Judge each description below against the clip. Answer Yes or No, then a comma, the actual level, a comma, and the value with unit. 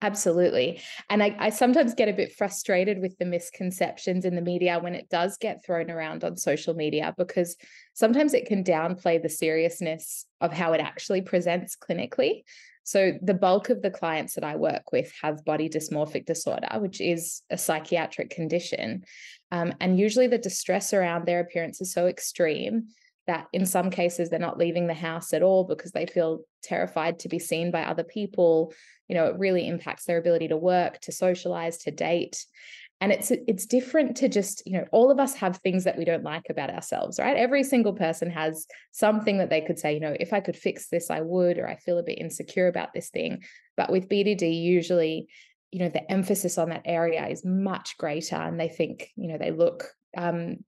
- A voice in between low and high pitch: Yes, medium, 175 Hz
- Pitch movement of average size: Yes, average, 3.2 semitones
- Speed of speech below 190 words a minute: No, average, 200 wpm